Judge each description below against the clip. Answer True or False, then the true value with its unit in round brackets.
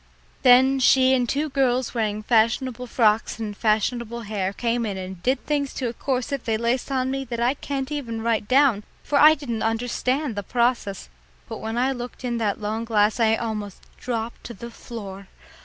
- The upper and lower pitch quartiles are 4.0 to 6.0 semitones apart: False (2.9 semitones)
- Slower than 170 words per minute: False (190 wpm)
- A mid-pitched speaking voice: False (235 Hz)